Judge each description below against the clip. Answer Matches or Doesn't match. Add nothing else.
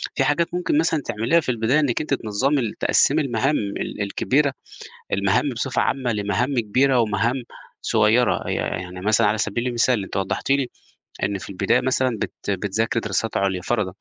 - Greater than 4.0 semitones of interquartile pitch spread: Matches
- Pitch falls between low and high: Doesn't match